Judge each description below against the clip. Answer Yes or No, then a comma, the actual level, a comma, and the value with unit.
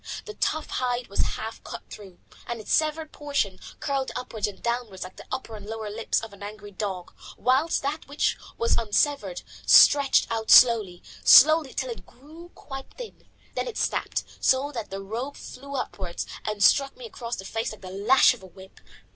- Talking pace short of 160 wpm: No, average, 190 wpm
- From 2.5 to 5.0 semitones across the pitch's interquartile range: No, wide, 5.4 semitones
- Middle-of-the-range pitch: No, high, 235 Hz